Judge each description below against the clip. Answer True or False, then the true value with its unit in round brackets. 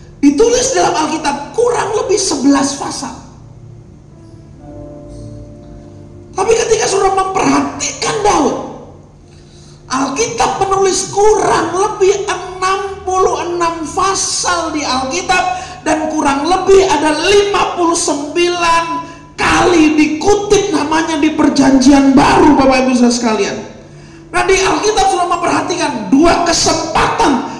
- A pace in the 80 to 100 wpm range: True (90 wpm)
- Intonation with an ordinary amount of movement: True (4.1 semitones)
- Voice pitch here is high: True (350 Hz)